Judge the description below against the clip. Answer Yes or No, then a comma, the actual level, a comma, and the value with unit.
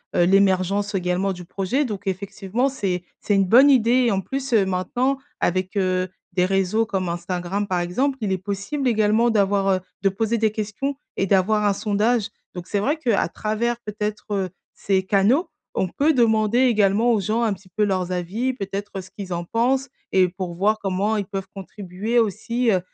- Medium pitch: No, high, 205 Hz